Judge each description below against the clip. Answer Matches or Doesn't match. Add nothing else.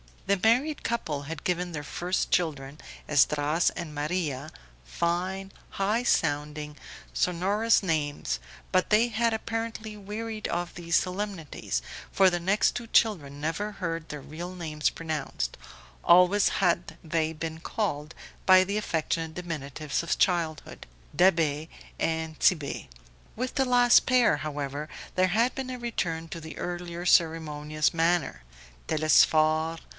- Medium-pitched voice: Matches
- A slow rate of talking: Matches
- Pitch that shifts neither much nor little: Matches